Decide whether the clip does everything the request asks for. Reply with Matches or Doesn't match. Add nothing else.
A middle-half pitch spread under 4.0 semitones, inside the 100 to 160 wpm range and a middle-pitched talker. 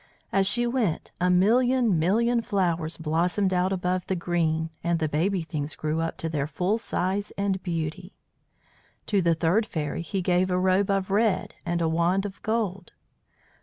Doesn't match